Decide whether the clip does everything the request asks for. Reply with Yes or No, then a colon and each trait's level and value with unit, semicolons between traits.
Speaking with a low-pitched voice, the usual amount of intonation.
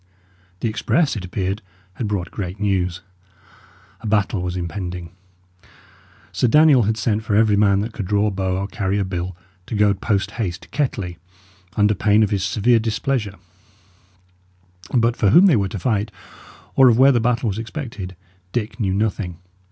Yes: low, 105 Hz; average, 3.1 semitones